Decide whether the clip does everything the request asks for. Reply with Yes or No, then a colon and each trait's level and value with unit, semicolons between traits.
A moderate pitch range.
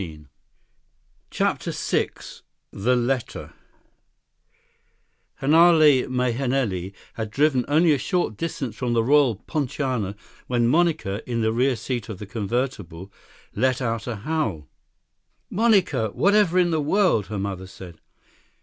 No: wide, 6.0 semitones